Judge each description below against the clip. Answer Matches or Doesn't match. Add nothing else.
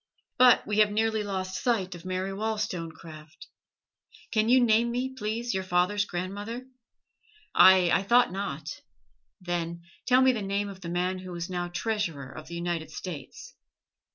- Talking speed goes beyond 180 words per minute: Doesn't match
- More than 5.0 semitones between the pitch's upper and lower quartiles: Doesn't match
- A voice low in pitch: Doesn't match